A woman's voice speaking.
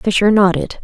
Yes: female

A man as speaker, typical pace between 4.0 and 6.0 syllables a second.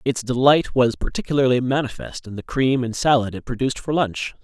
Yes: male; 5.6 syllables/s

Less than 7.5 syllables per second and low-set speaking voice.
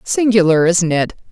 No: 4.8 syllables/s; medium, 185 Hz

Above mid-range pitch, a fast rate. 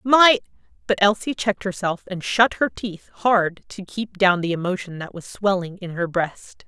No: high, 195 Hz; average, 180 wpm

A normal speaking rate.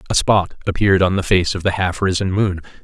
No: fast, 235 wpm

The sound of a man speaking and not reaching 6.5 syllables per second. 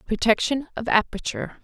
No: female; 5.8 syllables/s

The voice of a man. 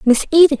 No: female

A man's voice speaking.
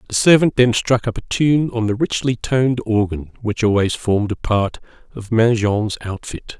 Yes: male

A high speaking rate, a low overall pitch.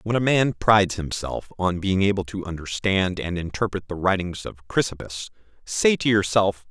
No: average, 170 wpm; very low, 95 Hz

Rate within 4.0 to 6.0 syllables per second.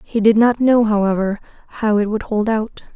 Yes: 5.2 syllables/s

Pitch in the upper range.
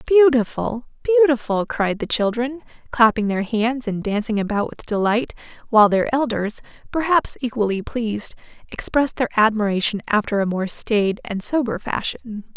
Yes: high, 230 Hz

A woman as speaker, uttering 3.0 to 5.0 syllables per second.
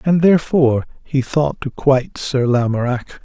No: male; 4.7 syllables/s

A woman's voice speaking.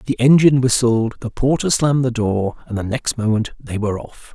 No: male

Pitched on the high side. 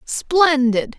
Yes: very high, 285 Hz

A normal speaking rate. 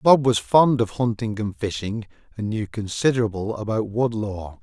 Yes: average, 170 wpm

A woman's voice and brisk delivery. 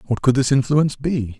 No: male; fast, 215 wpm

